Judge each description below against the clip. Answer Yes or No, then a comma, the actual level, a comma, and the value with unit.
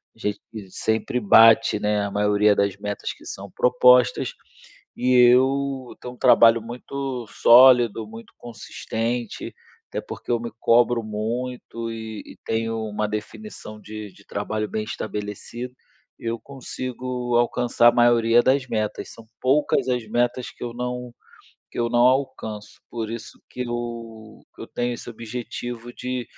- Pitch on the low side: Yes, low, 120 Hz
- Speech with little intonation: Yes, narrow, 2.3 semitones